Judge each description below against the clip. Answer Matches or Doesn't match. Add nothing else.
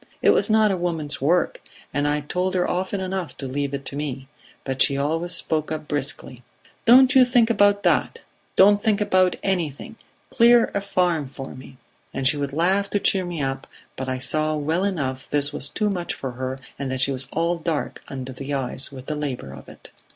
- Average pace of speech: Doesn't match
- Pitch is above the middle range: Doesn't match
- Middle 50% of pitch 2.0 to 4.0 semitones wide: Doesn't match